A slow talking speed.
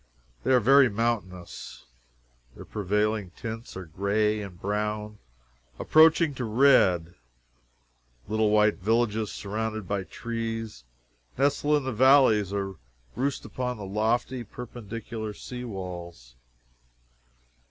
Yes: slow, 110 wpm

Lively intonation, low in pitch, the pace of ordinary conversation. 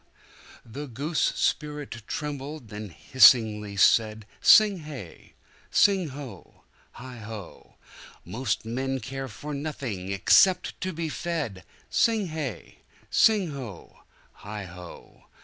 No: wide, 6.0 semitones; low, 130 Hz; slow, 95 wpm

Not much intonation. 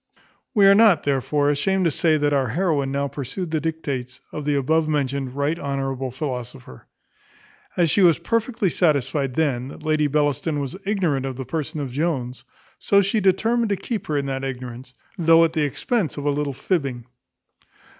No: average, 3.7 semitones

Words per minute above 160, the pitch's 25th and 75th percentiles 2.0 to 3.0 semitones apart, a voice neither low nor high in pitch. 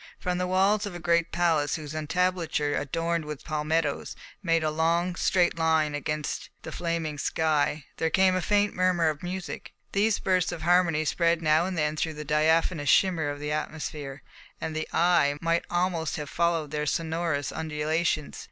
Yes: average, 170 wpm; narrow, 2.4 semitones; medium, 160 Hz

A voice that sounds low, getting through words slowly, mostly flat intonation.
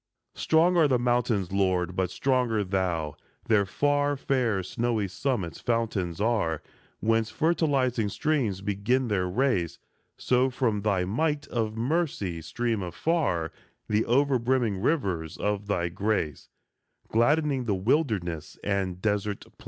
No: low, 110 Hz; slow, 130 wpm; wide, 5.5 semitones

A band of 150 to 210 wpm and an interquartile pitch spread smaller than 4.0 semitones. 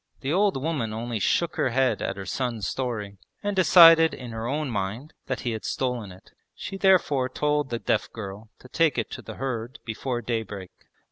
No: average, 195 wpm; average, 4.9 semitones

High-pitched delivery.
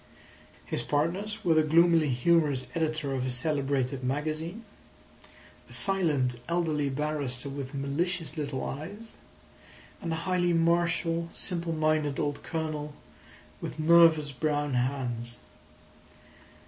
No: medium, 155 Hz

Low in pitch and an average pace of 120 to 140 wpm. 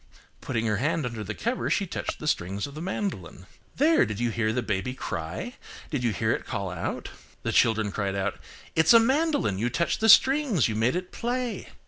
No: low, 120 Hz; average, 200 wpm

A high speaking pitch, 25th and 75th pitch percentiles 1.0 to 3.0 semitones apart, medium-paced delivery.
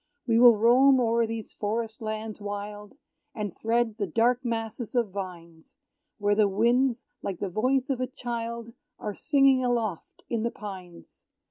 Yes: high, 225 Hz; average, 2.7 semitones; average, 155 wpm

